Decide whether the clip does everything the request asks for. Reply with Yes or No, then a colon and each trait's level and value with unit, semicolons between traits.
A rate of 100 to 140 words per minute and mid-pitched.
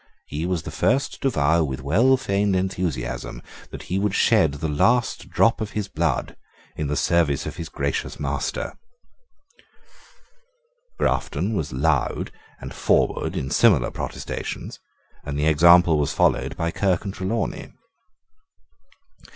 No: slow, 135 wpm; very low, 85 Hz